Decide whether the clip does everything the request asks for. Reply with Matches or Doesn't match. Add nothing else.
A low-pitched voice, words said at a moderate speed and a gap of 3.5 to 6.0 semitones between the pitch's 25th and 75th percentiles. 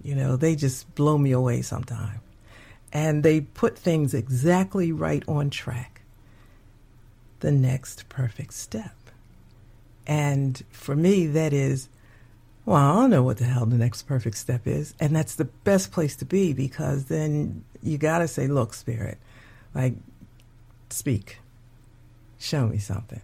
Matches